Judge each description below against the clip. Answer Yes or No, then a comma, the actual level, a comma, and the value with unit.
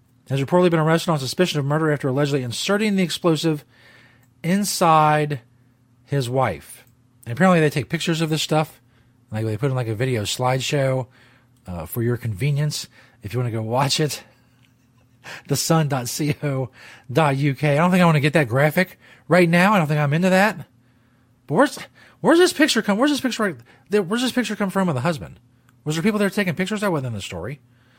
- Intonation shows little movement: No, wide, 5.6 semitones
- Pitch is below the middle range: No, medium, 145 Hz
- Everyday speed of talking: Yes, average, 195 wpm